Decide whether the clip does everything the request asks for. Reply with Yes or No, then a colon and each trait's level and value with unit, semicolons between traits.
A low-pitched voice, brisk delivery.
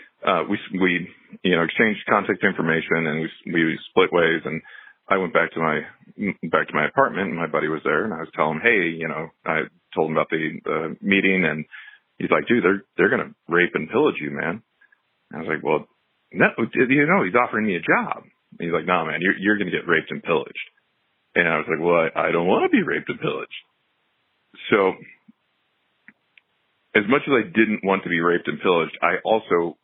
Yes: very low, 85 Hz; fast, 225 wpm